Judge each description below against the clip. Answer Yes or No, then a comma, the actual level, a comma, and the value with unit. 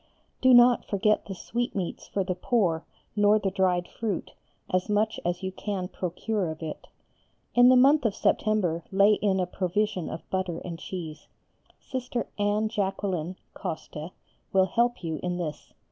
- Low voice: No, high, 195 Hz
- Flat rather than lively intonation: No, average, 3.4 semitones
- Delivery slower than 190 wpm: Yes, average, 160 wpm